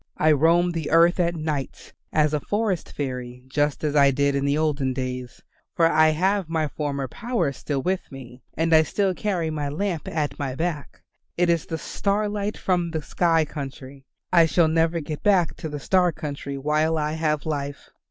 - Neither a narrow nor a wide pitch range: Yes, average, 3.2 semitones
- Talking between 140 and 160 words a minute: No, average, 190 wpm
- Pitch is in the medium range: Yes, medium, 155 Hz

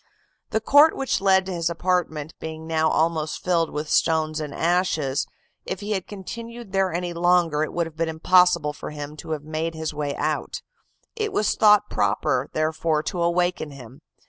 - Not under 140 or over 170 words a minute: No, average, 180 wpm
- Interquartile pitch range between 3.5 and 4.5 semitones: No, average, 3.0 semitones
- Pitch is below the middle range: No, medium, 165 Hz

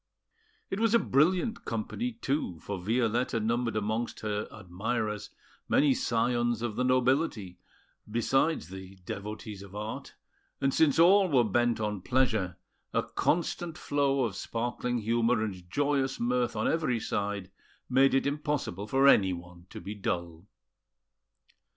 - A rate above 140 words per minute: No, slow, 135 wpm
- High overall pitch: No, low, 115 Hz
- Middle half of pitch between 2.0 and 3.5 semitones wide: No, average, 4.7 semitones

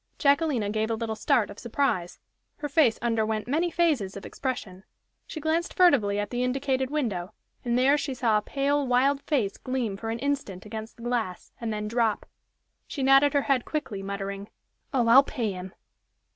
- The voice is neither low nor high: No, high, 240 Hz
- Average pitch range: Yes, average, 4.8 semitones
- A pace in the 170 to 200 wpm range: Yes, average, 180 wpm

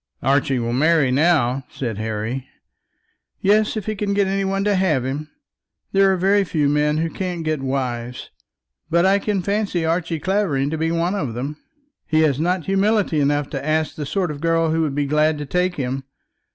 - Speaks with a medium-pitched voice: Yes, medium, 160 Hz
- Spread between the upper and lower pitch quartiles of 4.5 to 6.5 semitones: Yes, wide, 5.4 semitones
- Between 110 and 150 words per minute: No, average, 195 wpm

